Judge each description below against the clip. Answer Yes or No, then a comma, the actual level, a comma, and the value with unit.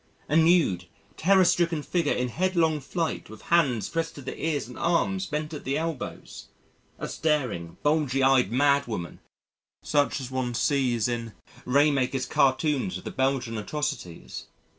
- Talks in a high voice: No, medium, 140 Hz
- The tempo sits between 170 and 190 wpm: No, average, 150 wpm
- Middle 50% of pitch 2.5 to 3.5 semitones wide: No, average, 4.5 semitones